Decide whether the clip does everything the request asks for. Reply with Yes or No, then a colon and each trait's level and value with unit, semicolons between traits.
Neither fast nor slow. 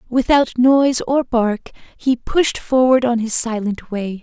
Yes: average, 155 wpm